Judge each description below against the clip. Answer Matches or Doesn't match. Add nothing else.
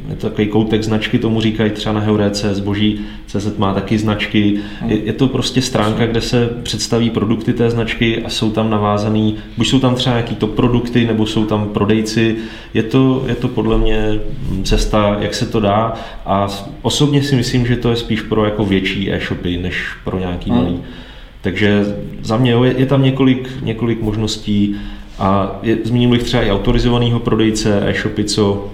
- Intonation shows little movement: Matches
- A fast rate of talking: Matches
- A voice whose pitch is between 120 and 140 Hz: Doesn't match